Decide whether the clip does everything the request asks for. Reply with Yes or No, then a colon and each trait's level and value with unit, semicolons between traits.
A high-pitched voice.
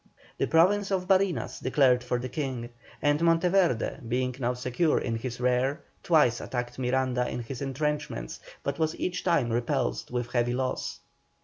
No: low, 130 Hz